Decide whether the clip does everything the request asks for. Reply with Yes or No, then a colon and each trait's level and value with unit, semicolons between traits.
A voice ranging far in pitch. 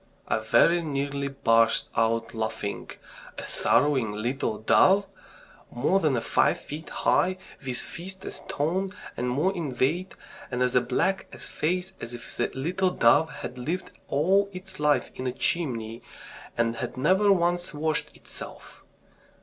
Yes: wide, 6.8 semitones